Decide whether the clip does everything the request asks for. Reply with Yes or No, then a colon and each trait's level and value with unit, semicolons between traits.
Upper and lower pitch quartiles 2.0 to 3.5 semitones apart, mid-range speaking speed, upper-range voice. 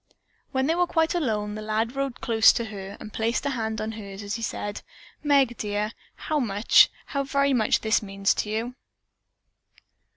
No: average, 4.3 semitones; average, 185 wpm; high, 225 Hz